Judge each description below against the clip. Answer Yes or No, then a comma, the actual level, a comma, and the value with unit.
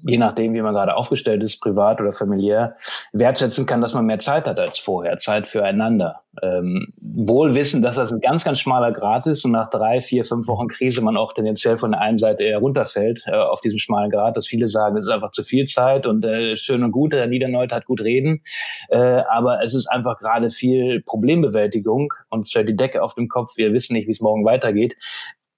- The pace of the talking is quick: Yes, fast, 220 wpm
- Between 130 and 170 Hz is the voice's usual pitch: No, low, 115 Hz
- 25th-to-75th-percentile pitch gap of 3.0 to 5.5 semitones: No, narrow, 2.6 semitones